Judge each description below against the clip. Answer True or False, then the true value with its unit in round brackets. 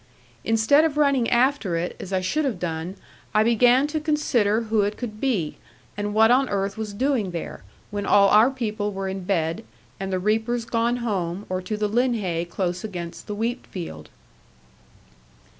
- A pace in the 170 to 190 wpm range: True (175 wpm)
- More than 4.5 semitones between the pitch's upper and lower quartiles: False (4.2 semitones)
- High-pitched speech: True (210 Hz)